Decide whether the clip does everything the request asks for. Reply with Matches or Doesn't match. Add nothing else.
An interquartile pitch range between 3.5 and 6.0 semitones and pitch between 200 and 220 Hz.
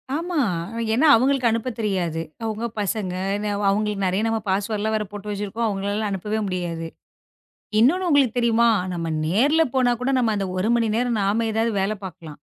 Doesn't match